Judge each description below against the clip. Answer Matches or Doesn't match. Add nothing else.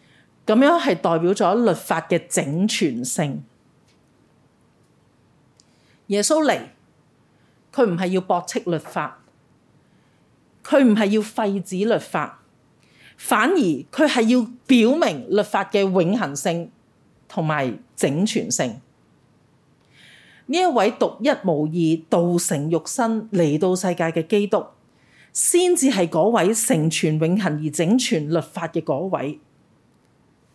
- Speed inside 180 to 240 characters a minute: Doesn't match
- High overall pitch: Matches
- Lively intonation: Matches